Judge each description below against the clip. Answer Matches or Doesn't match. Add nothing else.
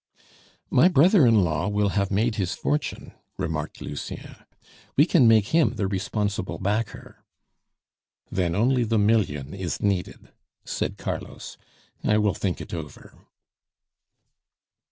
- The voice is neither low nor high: Doesn't match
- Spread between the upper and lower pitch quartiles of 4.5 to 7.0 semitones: Doesn't match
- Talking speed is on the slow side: Matches